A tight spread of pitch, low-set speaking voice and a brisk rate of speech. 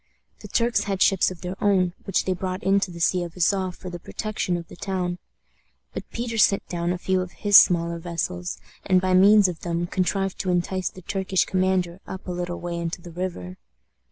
No: narrow, 1.6 semitones; medium, 185 Hz; fast, 210 wpm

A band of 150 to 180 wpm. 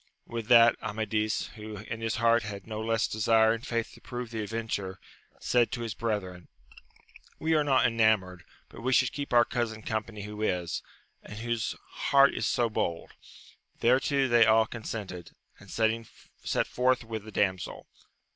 Yes: average, 165 wpm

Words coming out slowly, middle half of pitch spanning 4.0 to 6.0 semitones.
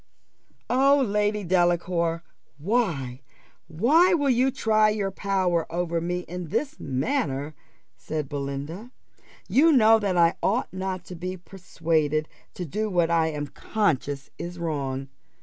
Yes: slow, 130 wpm; average, 5.1 semitones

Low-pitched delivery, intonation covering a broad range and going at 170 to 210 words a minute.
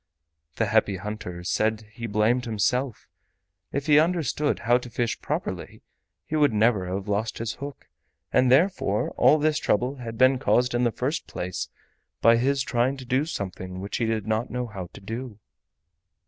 No: low, 120 Hz; average, 3.8 semitones; average, 175 wpm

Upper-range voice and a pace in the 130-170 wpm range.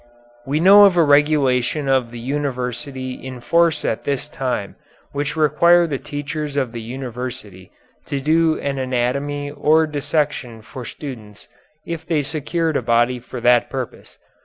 No: medium, 140 Hz; average, 150 wpm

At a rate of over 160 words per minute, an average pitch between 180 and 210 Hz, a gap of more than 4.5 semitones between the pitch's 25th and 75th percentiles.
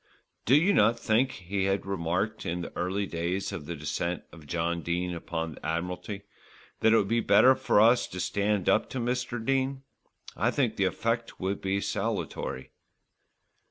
No: average, 175 wpm; low, 100 Hz; average, 5.1 semitones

